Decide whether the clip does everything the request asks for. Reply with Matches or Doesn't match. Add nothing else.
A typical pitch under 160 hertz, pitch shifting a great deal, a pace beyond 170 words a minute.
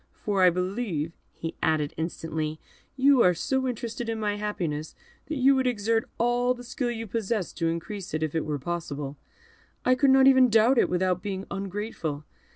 Doesn't match